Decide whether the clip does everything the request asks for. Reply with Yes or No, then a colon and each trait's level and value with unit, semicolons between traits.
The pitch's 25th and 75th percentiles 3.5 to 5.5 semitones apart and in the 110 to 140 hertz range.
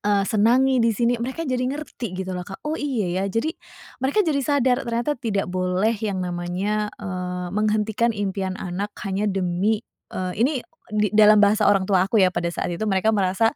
No: average, 3.8 semitones; high, 210 Hz